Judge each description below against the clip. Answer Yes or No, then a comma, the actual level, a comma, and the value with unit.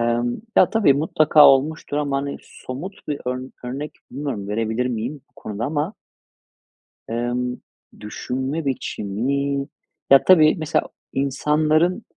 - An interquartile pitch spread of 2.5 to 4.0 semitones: Yes, average, 3.5 semitones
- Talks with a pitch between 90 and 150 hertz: Yes, medium, 140 Hz